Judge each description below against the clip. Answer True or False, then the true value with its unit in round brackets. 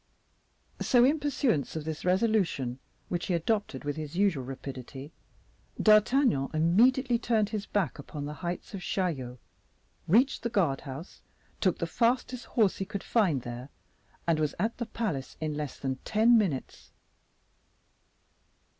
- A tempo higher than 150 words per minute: False (145 wpm)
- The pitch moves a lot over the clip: True (7.5 semitones)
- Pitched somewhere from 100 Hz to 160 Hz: False (180 Hz)